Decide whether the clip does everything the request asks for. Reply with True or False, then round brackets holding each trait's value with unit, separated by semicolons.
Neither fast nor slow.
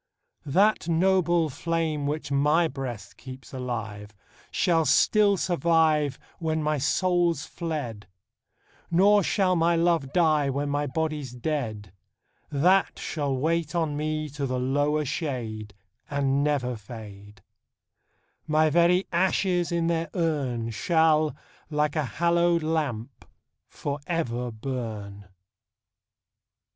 False (110 wpm)